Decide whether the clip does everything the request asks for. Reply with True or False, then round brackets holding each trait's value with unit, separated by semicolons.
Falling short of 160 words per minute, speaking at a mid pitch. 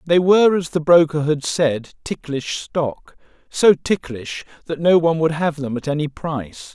False (180 wpm; 155 Hz)